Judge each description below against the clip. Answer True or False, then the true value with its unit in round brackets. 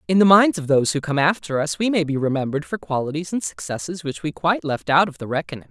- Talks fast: True (265 wpm)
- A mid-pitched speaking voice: True (155 Hz)